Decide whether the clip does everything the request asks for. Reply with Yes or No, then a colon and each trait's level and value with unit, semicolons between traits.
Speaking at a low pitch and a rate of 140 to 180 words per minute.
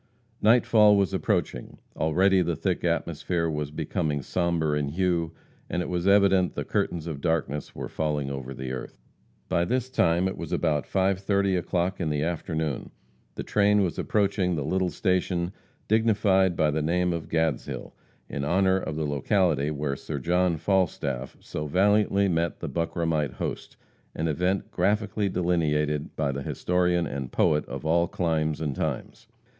Yes: very low, 85 Hz; average, 160 wpm